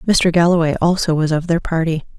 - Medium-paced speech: Yes, average, 190 wpm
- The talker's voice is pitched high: No, medium, 165 Hz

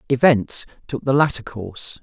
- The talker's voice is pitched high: No, low, 125 Hz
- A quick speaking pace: No, average, 150 wpm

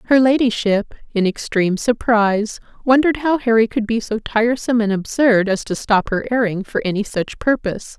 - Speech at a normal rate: Yes, average, 175 wpm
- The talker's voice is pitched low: No, high, 225 Hz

